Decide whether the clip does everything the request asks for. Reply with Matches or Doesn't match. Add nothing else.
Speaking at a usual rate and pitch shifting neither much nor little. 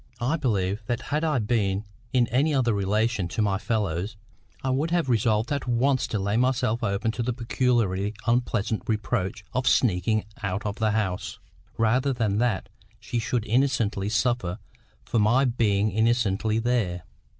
Matches